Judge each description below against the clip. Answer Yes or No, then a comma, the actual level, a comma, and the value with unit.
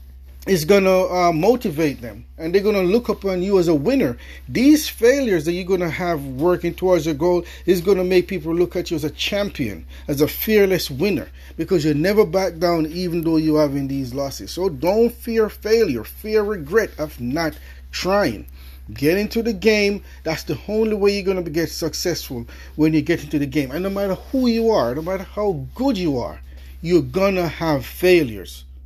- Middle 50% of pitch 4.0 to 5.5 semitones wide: Yes, average, 4.7 semitones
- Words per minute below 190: No, fast, 205 wpm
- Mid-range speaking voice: Yes, medium, 175 Hz